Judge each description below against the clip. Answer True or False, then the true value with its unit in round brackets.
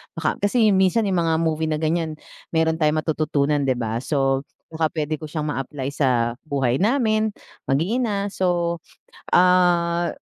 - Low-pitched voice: False (160 Hz)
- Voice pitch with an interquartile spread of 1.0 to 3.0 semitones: False (3.8 semitones)